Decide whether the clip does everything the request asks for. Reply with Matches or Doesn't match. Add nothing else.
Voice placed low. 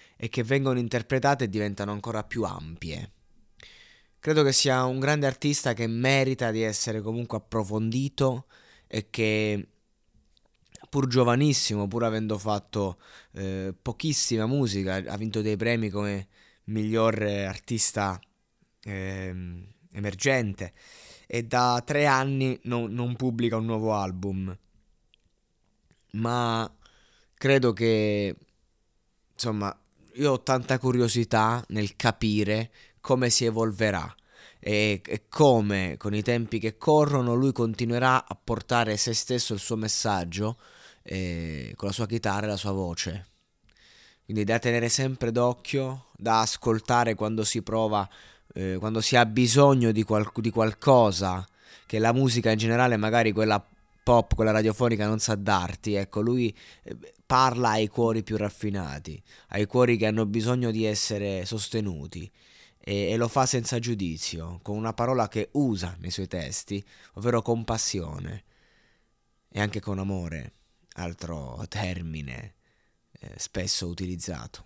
Matches